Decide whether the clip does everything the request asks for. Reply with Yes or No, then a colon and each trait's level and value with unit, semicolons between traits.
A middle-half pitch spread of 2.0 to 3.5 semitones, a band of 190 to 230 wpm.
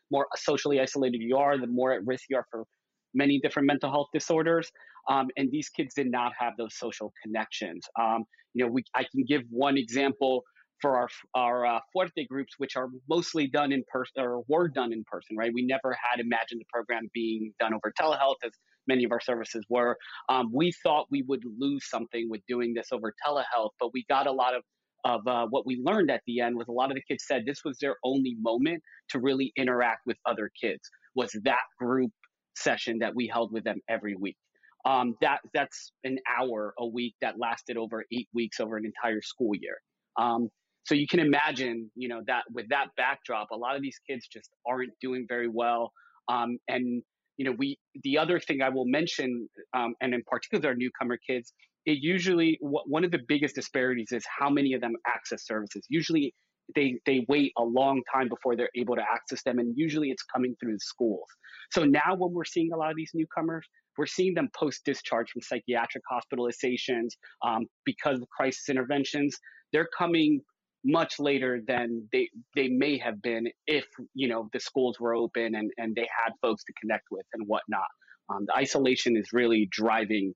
Yes: average, 3.1 semitones; average, 200 wpm